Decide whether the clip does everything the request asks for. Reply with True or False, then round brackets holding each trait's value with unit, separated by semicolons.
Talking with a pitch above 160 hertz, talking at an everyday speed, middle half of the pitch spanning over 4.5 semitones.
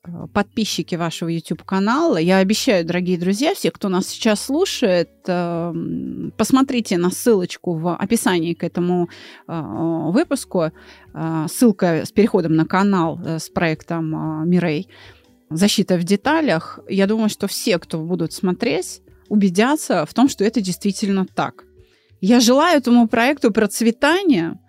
True (190 Hz; 120 wpm; 5.2 semitones)